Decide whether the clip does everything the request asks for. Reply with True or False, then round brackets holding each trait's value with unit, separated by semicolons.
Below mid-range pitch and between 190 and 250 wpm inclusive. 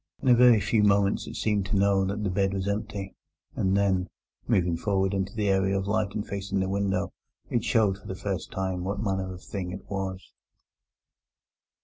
True (100 Hz; 200 wpm)